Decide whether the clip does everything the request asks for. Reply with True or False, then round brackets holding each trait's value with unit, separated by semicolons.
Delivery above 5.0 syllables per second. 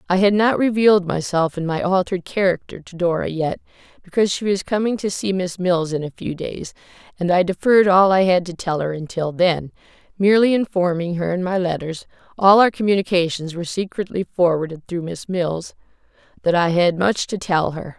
False (4.5 syllables/s)